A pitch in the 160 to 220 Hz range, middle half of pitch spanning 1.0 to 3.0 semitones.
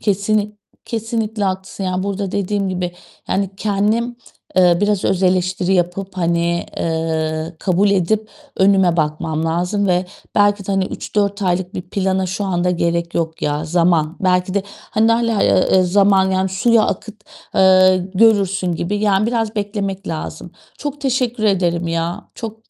Yes: high, 190 Hz; narrow, 2.6 semitones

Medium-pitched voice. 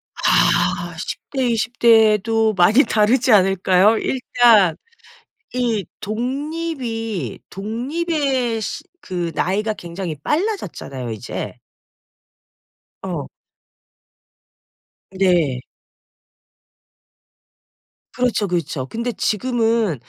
No: high, 220 Hz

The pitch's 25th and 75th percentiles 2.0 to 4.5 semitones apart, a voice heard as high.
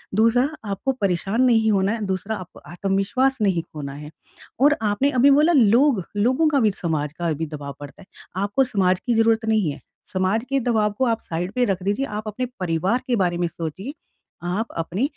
No: wide, 5.5 semitones; high, 205 Hz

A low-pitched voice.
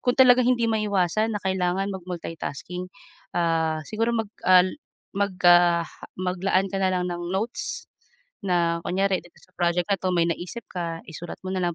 No: medium, 185 Hz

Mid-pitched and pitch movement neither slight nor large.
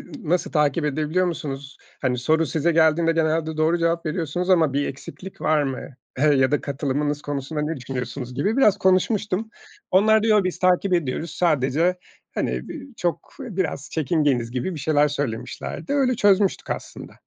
Yes: medium, 160 Hz; average, 4.3 semitones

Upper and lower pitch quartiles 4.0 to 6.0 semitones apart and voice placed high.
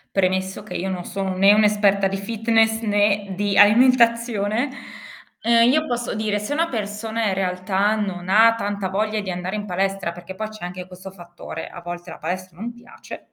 No: average, 2.8 semitones; high, 205 Hz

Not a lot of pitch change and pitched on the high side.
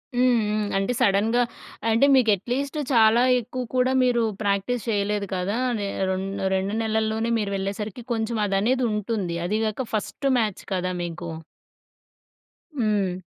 No: average, 3.1 semitones; high, 215 Hz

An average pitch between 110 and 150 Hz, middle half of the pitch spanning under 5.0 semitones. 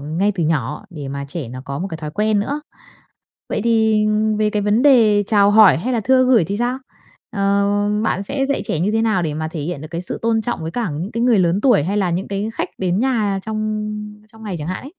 No: high, 205 Hz; average, 4.6 semitones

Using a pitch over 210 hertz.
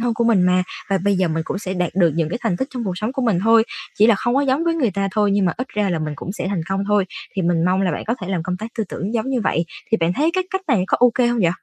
No: high, 200 Hz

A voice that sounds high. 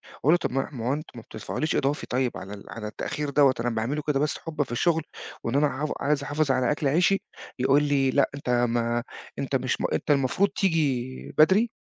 No: medium, 140 Hz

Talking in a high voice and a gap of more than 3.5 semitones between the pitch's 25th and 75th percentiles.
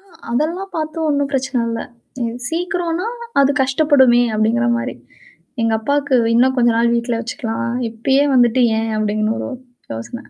Yes: very high, 250 Hz; average, 3.9 semitones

